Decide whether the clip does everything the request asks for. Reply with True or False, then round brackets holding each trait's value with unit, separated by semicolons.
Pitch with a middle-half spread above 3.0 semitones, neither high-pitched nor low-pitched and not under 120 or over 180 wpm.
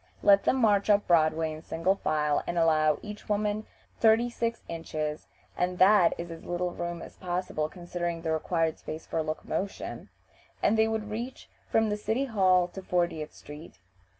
True (4.4 semitones; 180 Hz; 170 wpm)